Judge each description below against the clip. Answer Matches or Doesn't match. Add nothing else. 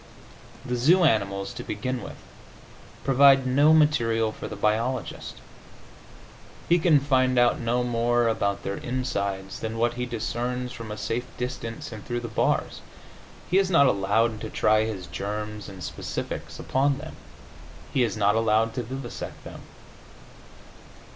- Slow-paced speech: Doesn't match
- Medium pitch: Doesn't match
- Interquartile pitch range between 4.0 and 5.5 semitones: Doesn't match